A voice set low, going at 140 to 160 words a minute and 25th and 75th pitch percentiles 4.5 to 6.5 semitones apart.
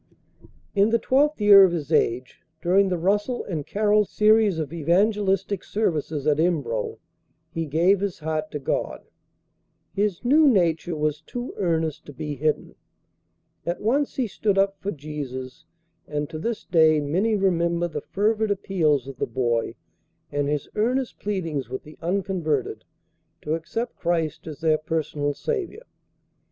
No: medium, 170 Hz; average, 150 wpm; average, 5.3 semitones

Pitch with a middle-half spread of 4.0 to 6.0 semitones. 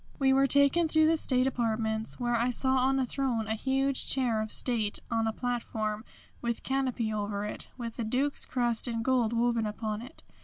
No: average, 3.1 semitones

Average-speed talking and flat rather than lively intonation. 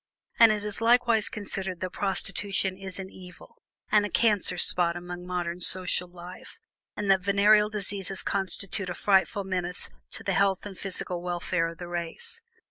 Yes: average, 165 wpm; narrow, 2.3 semitones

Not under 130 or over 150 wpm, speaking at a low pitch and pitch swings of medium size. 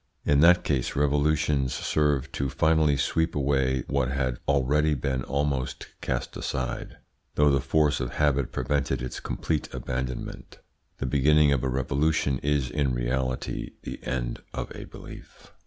No: average, 145 wpm; very low, 70 Hz; narrow, 2.3 semitones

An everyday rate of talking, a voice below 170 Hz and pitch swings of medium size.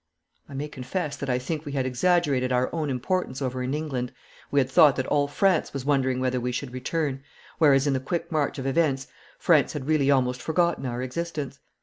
No: fast, 210 wpm; medium, 140 Hz; average, 3.0 semitones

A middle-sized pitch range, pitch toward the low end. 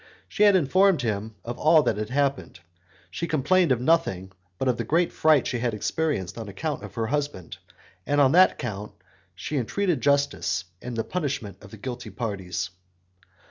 No: wide, 6.4 semitones; low, 130 Hz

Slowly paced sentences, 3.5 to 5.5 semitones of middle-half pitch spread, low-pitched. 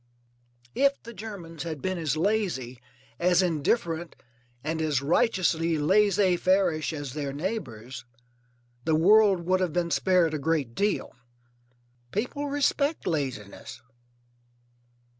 No: slow, 115 wpm; average, 4.7 semitones; medium, 170 Hz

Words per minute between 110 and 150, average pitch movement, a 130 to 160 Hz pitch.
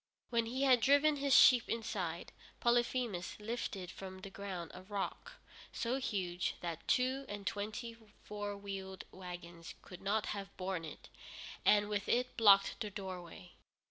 No: average, 145 wpm; average, 4.1 semitones; high, 205 Hz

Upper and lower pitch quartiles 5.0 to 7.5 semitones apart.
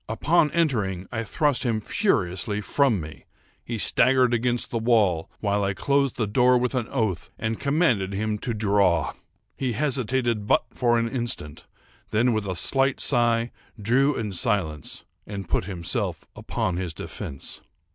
No: average, 4.1 semitones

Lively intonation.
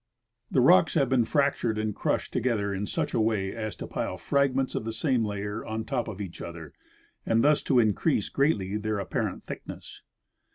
No: average, 4.0 semitones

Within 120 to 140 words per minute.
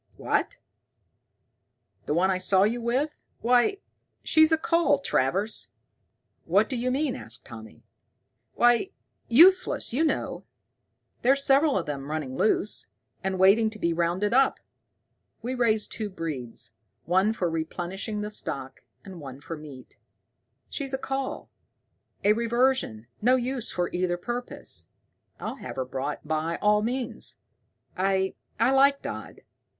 Yes: slow, 135 wpm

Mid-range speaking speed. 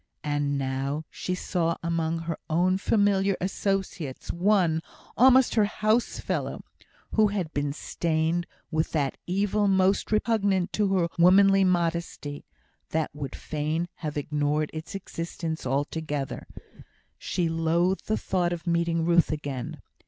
No: slow, 125 wpm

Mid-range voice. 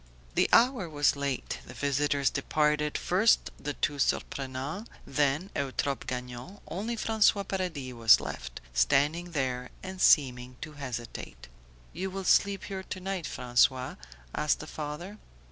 Yes: medium, 145 Hz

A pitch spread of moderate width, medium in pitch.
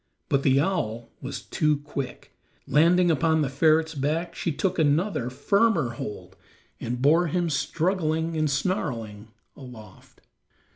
Yes: average, 3.9 semitones; medium, 155 Hz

